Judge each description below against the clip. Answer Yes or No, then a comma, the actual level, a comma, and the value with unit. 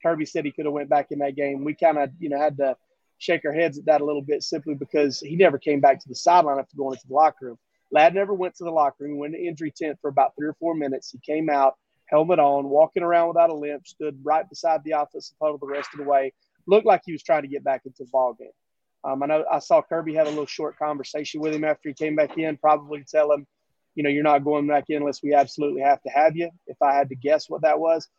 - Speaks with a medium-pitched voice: Yes, medium, 150 Hz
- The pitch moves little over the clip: Yes, narrow, 1.9 semitones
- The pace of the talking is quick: Yes, fast, 285 wpm